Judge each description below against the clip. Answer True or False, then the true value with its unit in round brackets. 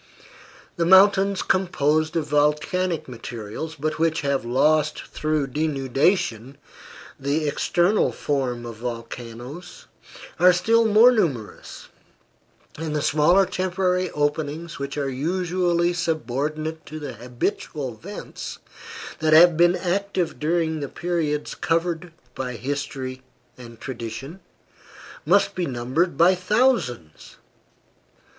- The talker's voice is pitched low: False (155 Hz)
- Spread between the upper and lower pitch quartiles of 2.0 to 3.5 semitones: False (4.7 semitones)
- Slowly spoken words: True (110 wpm)